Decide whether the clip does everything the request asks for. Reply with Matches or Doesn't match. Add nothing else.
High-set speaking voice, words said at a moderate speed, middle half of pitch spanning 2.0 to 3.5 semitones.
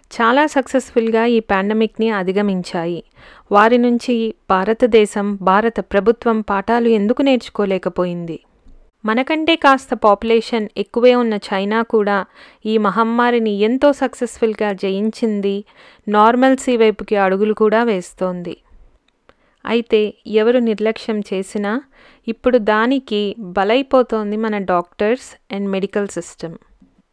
Matches